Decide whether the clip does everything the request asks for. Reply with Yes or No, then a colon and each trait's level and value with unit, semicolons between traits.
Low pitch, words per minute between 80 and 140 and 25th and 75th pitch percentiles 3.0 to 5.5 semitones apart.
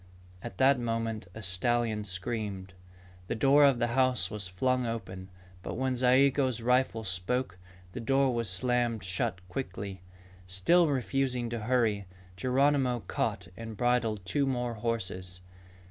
Yes: low, 115 Hz; slow, 135 wpm; average, 4.4 semitones